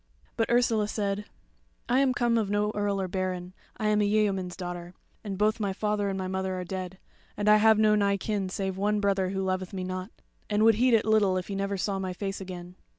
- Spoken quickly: Yes, fast, 230 wpm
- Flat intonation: Yes, narrow, 2.1 semitones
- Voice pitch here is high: Yes, high, 200 Hz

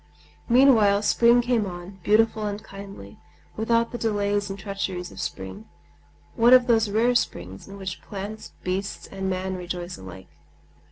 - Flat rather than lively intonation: No, average, 3.2 semitones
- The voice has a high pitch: Yes, high, 200 Hz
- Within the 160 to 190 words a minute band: No, average, 145 wpm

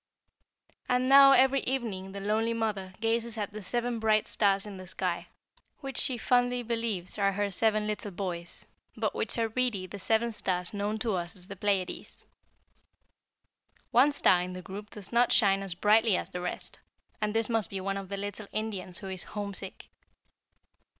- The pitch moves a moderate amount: Yes, average, 3.1 semitones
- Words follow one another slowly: No, average, 175 wpm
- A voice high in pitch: Yes, high, 210 Hz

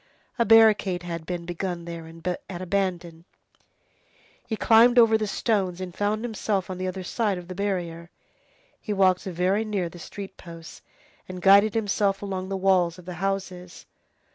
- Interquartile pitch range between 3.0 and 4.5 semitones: No, narrow, 2.6 semitones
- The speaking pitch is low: No, medium, 185 Hz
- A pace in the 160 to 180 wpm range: Yes, average, 165 wpm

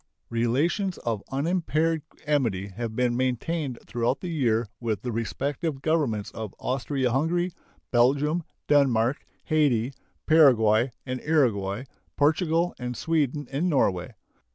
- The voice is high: No, low, 135 Hz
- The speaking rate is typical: No, slow, 115 wpm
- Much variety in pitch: No, average, 5.0 semitones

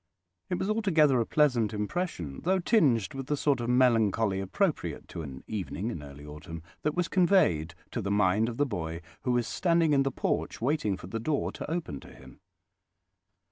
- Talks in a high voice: No, low, 120 Hz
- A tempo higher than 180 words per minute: Yes, average, 190 wpm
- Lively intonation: Yes, wide, 8.4 semitones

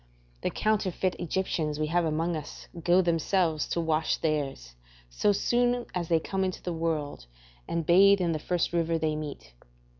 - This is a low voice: No, medium, 165 Hz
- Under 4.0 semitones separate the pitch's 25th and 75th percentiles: Yes, average, 3.1 semitones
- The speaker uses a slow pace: No, average, 170 wpm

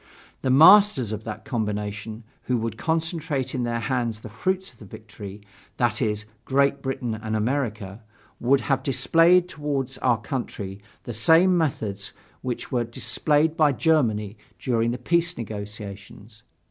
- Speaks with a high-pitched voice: No, low, 120 Hz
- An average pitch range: Yes, average, 5.0 semitones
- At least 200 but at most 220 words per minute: No, average, 145 wpm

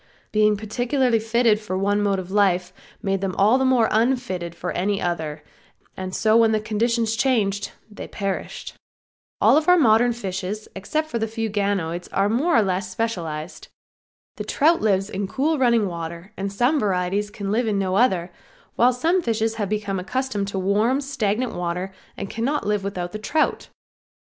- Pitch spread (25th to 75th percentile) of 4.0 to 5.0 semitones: No, average, 3.5 semitones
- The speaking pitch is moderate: No, high, 210 Hz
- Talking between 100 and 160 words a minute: No, average, 170 wpm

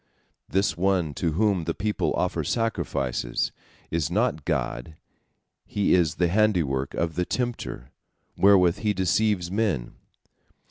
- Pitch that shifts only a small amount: No, average, 4.8 semitones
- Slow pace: Yes, slow, 125 wpm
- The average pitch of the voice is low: Yes, very low, 90 Hz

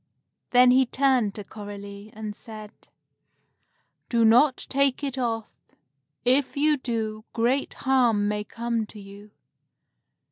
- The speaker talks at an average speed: No, slow, 120 wpm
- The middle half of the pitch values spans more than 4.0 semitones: No, average, 3.6 semitones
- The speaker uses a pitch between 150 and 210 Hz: No, high, 230 Hz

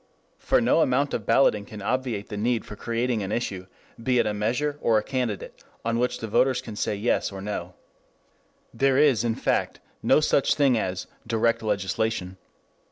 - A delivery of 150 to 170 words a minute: No, average, 180 wpm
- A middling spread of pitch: Yes, average, 3.4 semitones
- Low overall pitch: Yes, low, 115 Hz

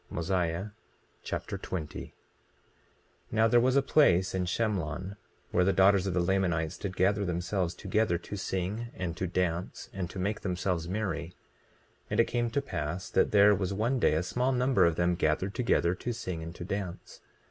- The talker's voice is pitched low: Yes, very low, 95 Hz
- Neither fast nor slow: Yes, average, 185 wpm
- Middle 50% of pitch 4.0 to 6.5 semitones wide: No, average, 3.2 semitones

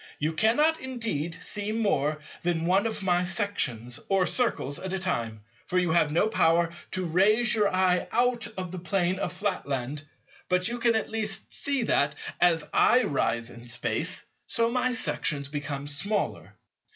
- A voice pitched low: No, medium, 185 Hz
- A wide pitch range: Yes, wide, 6.4 semitones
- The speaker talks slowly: No, average, 165 wpm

